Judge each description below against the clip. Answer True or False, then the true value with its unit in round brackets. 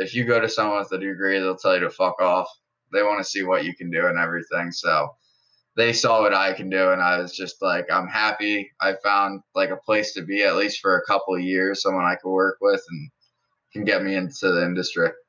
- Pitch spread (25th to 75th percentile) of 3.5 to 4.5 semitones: False (2.4 semitones)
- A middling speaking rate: False (250 wpm)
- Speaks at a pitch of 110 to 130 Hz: False (95 Hz)